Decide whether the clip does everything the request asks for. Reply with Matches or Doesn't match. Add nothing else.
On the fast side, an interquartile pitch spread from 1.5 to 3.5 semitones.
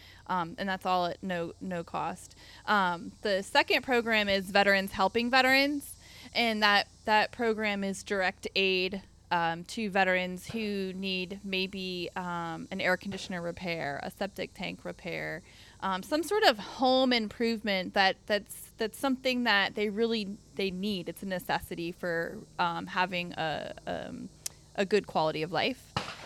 Doesn't match